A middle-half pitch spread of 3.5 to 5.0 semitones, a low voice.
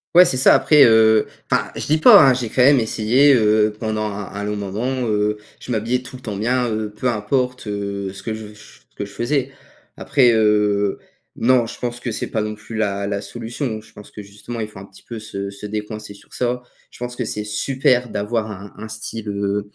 No: average, 2.9 semitones; low, 110 Hz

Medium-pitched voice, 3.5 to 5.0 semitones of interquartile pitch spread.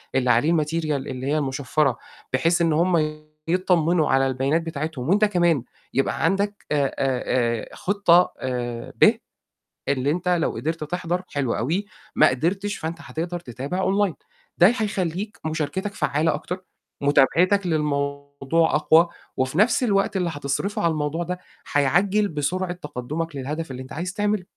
Yes: medium, 160 Hz; average, 4.2 semitones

